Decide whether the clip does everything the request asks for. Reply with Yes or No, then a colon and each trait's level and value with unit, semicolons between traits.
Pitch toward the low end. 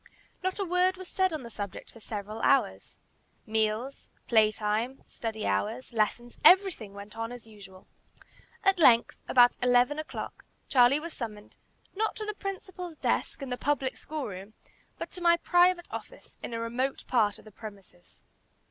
No: high, 245 Hz